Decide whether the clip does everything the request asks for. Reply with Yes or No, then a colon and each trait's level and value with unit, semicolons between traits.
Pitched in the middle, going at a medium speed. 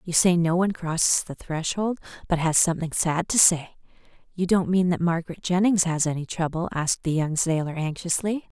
Yes: medium, 170 Hz; average, 190 wpm